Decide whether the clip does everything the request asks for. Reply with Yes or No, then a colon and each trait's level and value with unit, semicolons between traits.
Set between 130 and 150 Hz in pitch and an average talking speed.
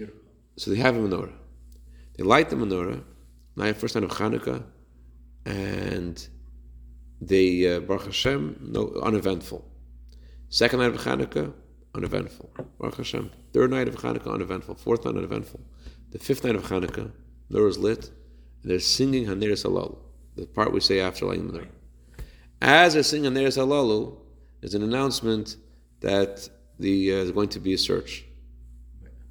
No: very low, 85 Hz; average, 150 wpm